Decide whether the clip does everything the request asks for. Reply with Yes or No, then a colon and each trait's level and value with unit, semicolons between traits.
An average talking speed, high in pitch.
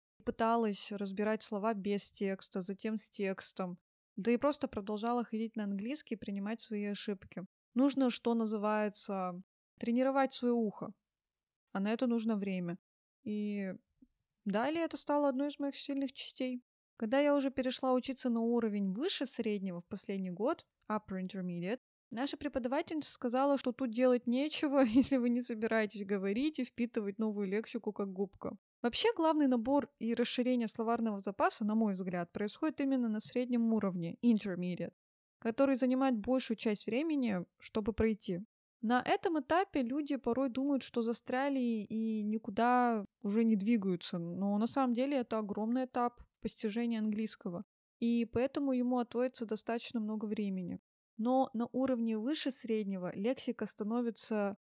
Yes: average, 145 wpm; high, 230 Hz